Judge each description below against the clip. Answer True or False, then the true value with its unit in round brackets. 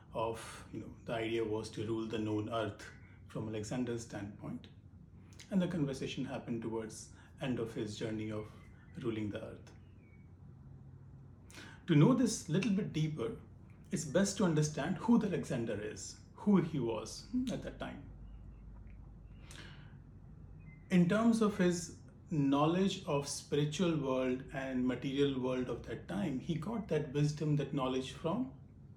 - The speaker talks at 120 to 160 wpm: True (140 wpm)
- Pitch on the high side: False (135 Hz)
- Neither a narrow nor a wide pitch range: False (6.5 semitones)